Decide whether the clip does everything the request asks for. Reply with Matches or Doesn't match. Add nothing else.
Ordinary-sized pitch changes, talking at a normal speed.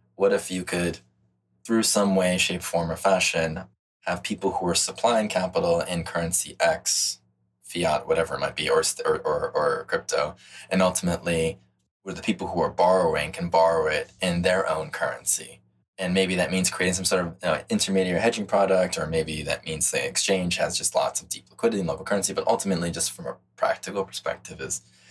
Matches